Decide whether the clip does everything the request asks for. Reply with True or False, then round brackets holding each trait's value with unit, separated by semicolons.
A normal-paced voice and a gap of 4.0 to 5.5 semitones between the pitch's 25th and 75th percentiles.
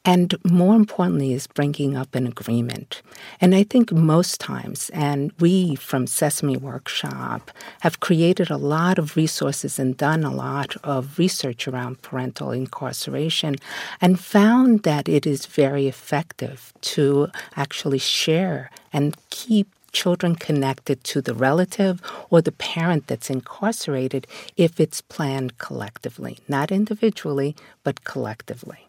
False (130 wpm; 4.6 semitones)